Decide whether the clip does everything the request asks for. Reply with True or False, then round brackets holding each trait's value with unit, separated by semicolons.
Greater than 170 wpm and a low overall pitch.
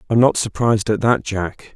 True (205 wpm; 110 Hz)